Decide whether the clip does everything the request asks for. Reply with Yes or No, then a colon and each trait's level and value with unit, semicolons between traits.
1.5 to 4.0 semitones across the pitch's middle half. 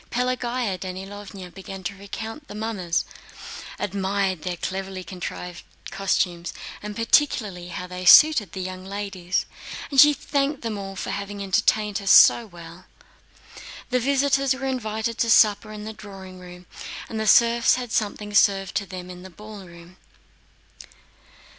Yes: average, 3.3 semitones